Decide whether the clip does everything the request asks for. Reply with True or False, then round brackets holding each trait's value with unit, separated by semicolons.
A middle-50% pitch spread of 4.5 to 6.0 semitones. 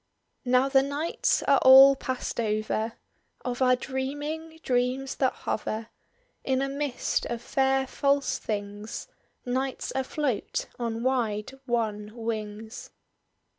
False (3.2 semitones)